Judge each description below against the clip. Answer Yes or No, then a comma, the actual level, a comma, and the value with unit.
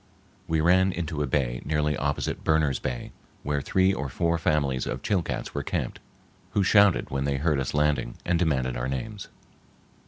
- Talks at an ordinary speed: Yes, average, 175 wpm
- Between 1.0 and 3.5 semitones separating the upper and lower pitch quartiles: No, average, 4.0 semitones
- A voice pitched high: No, very low, 75 Hz